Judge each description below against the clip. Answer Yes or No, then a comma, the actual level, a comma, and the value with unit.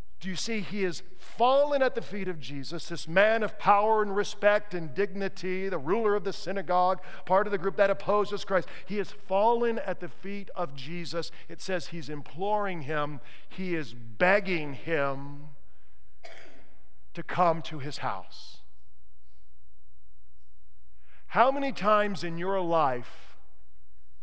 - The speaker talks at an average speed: Yes, average, 145 wpm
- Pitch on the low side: No, medium, 175 Hz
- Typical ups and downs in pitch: No, wide, 7.4 semitones